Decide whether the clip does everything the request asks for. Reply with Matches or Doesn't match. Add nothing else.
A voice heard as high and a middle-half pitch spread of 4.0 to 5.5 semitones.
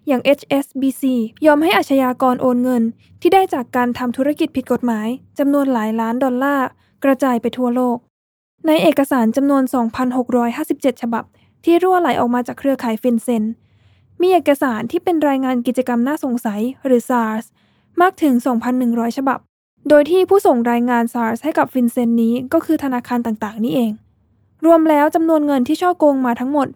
Doesn't match